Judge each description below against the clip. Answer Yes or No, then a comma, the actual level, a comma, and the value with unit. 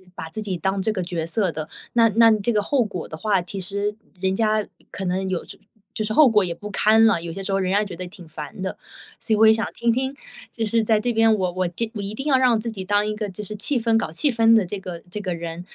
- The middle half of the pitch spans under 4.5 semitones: Yes, average, 3.4 semitones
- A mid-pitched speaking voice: No, high, 205 Hz